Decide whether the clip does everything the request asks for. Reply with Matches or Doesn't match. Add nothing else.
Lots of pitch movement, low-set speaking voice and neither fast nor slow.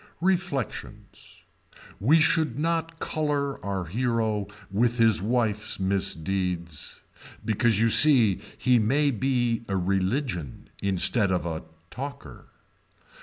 Doesn't match